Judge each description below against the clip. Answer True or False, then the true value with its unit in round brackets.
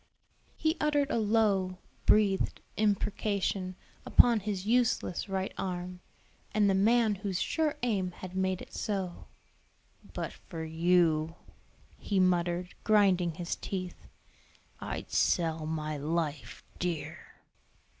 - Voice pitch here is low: False (185 Hz)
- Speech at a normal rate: False (115 wpm)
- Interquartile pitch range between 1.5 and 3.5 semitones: True (3.2 semitones)